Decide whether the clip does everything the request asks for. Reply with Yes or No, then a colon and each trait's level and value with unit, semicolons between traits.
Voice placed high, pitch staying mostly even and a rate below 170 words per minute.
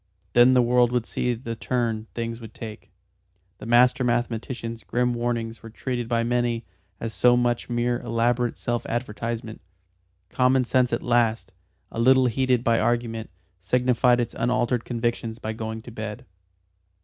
No: low, 120 Hz; narrow, 1.2 semitones; average, 150 wpm